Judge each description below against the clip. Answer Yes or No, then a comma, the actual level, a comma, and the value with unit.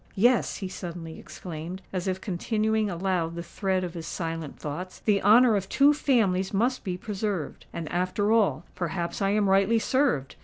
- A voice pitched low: No, high, 190 Hz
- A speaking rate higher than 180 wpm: No, average, 160 wpm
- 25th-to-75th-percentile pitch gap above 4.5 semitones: No, average, 3.6 semitones